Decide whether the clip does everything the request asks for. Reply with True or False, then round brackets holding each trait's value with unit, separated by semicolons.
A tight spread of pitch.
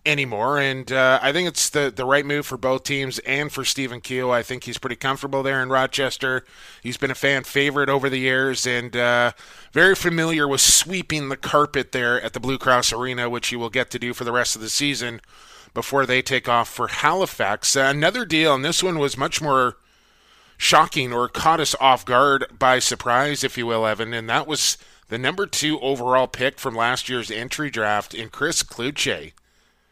True (2.3 semitones)